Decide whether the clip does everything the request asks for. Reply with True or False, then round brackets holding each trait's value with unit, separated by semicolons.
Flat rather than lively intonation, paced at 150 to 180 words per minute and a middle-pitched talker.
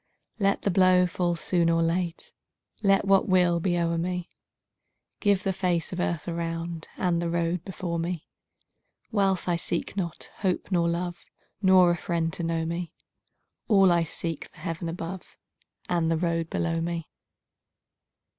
True (1.6 semitones; 155 wpm; 175 Hz)